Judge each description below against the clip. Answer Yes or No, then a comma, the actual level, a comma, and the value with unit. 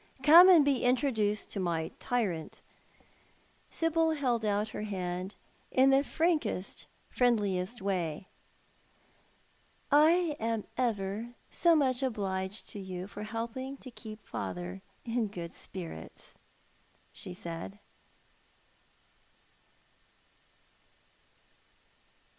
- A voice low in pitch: No, high, 220 Hz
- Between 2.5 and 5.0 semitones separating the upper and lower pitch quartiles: No, wide, 5.6 semitones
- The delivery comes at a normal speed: No, slow, 100 wpm